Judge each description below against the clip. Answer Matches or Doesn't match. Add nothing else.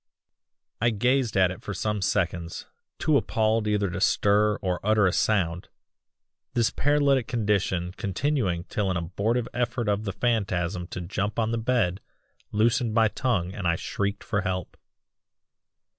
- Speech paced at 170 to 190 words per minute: Doesn't match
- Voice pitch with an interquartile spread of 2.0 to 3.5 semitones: Doesn't match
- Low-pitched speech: Matches